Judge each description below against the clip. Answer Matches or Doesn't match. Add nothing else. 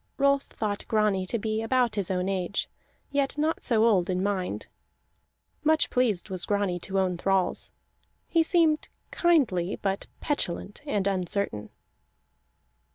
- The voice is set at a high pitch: Matches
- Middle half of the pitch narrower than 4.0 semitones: Doesn't match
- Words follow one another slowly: Matches